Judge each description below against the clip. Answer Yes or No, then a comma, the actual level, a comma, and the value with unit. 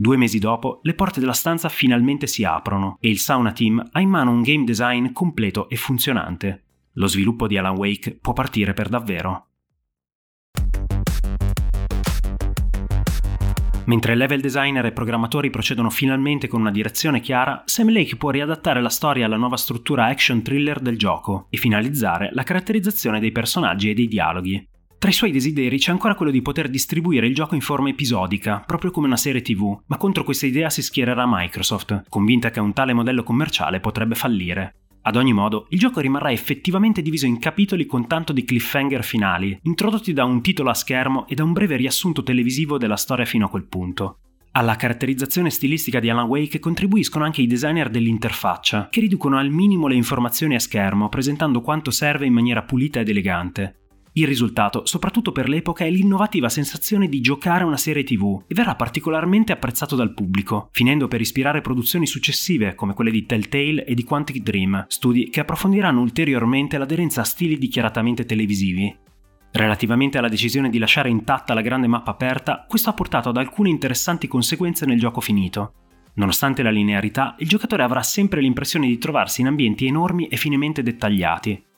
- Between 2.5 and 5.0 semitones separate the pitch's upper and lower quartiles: No, wide, 5.4 semitones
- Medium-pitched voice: No, low, 125 Hz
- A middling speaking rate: No, fast, 175 wpm